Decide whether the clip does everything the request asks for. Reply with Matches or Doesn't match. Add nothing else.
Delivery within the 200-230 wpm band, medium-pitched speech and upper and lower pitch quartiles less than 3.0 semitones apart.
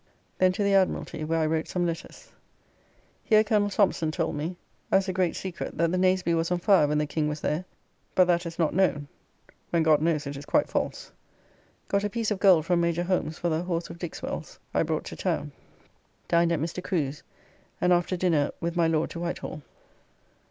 Matches